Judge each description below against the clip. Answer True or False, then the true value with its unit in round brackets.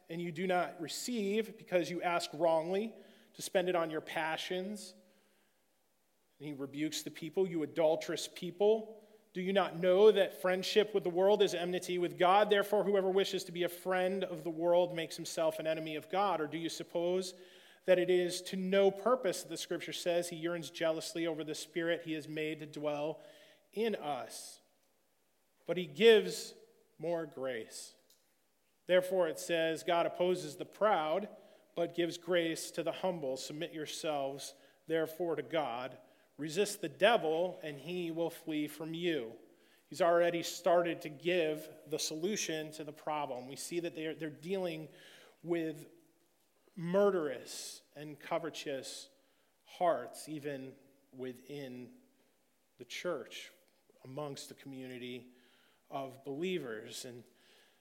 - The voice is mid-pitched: True (170 Hz)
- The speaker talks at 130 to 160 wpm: True (145 wpm)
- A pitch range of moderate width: True (3.0 semitones)